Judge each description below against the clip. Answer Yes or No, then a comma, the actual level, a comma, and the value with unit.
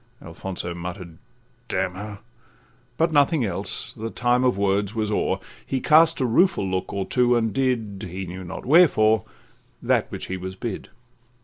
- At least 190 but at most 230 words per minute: No, average, 165 wpm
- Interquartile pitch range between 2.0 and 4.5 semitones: No, average, 5.0 semitones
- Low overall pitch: Yes, low, 105 Hz